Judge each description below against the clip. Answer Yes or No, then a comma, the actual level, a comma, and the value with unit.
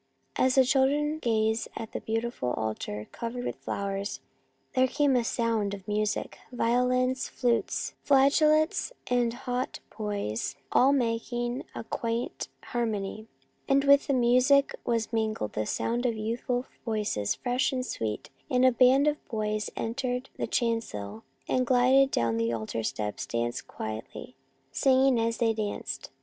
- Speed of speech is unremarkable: Yes, average, 145 wpm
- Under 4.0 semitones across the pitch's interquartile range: Yes, average, 3.4 semitones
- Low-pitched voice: No, high, 235 Hz